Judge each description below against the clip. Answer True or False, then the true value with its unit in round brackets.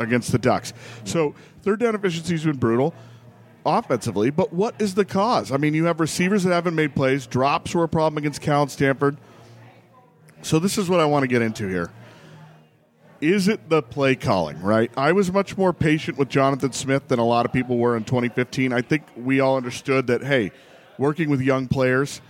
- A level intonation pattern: False (4.6 semitones)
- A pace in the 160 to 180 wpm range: False (205 wpm)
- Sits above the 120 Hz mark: True (140 Hz)